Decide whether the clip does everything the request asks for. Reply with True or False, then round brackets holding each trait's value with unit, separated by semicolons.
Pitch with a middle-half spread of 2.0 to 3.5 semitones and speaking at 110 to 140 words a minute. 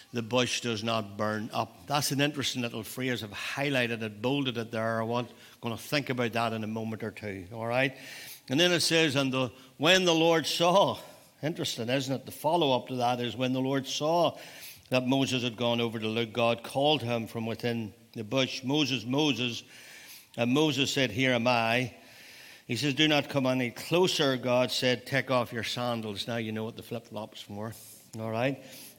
False (2.7 semitones; 205 wpm)